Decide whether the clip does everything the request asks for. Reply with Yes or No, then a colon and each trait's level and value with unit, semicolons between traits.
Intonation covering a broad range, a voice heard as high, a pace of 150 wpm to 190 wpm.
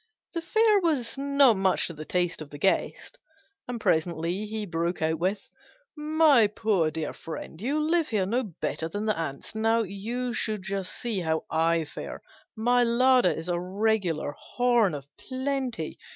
Yes: wide, 6.6 semitones; high, 210 Hz; average, 165 wpm